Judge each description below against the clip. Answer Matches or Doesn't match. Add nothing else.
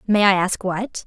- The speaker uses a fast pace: Matches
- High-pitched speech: Matches